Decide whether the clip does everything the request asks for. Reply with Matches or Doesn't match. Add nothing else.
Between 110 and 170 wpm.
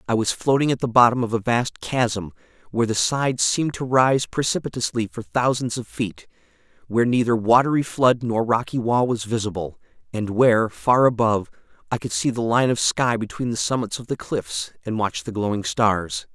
Doesn't match